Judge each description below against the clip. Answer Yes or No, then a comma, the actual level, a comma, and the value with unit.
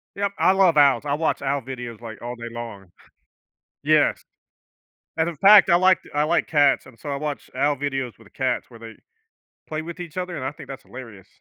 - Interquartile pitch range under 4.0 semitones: No, average, 5.1 semitones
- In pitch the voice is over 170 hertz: No, medium, 140 Hz